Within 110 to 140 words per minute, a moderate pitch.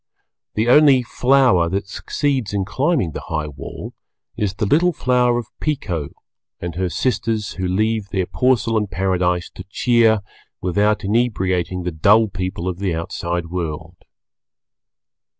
No: slow, 135 wpm; low, 100 Hz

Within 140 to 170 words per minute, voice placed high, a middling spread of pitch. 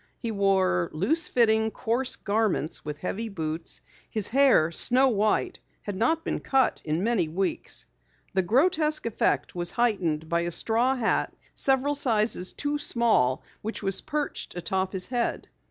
No: average, 150 wpm; high, 215 Hz; wide, 5.9 semitones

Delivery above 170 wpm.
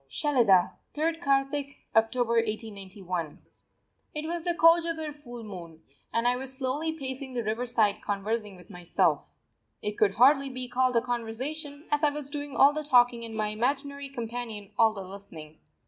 No: average, 160 wpm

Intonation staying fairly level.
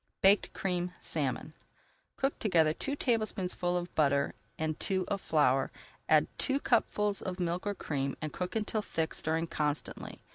No: average, 4.5 semitones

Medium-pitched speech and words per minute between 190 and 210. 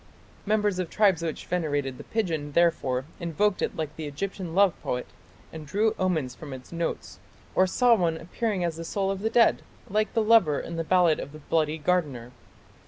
Yes: medium, 170 Hz; average, 195 wpm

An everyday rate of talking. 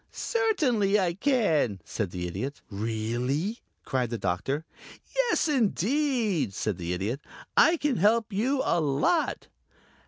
No: slow, 125 wpm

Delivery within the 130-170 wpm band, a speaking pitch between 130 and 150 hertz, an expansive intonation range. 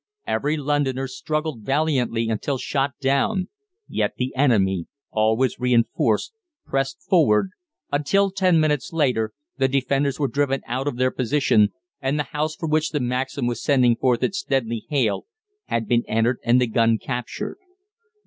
No: average, 150 wpm; low, 135 Hz; average, 3.7 semitones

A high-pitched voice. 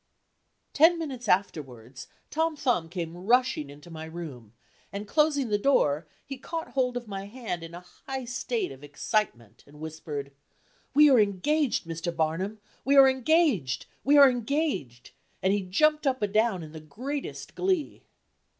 Yes: high, 205 Hz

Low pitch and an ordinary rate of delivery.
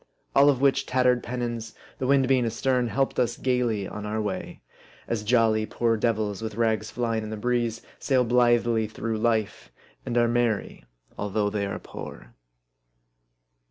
Yes: low, 115 Hz; average, 160 wpm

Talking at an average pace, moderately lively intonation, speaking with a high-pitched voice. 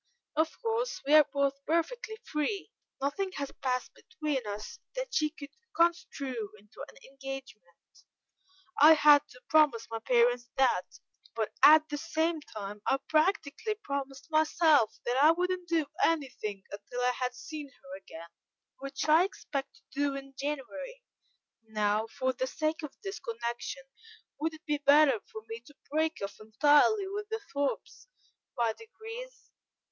Yes: average, 150 wpm; average, 4.5 semitones; very high, 285 Hz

